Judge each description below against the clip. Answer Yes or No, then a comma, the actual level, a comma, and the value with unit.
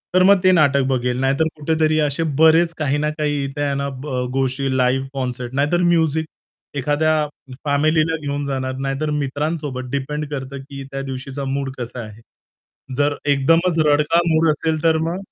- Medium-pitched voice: Yes, medium, 145 Hz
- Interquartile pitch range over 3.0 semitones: No, average, 2.7 semitones